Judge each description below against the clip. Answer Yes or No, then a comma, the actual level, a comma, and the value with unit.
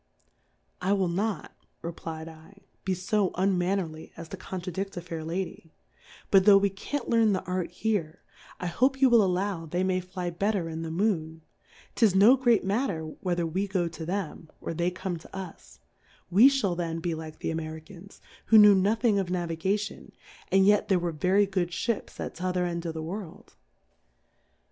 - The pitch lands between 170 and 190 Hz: Yes, medium, 185 Hz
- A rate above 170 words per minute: Yes, average, 185 wpm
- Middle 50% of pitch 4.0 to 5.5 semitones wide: No, average, 3.2 semitones